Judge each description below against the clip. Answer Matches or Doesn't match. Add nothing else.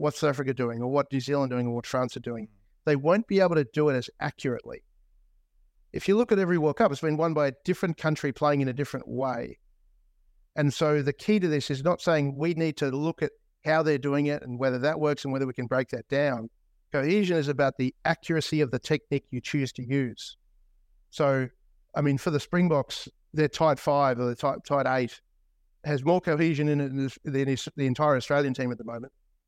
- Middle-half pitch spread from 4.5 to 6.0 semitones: Doesn't match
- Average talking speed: Doesn't match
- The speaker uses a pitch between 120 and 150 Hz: Matches